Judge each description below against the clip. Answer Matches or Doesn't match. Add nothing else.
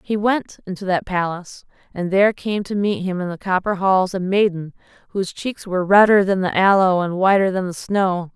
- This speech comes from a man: Doesn't match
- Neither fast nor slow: Doesn't match